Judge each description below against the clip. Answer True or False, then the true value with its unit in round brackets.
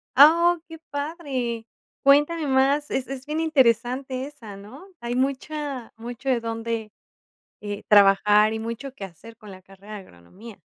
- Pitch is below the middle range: False (245 Hz)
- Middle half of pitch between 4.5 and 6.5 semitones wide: True (4.8 semitones)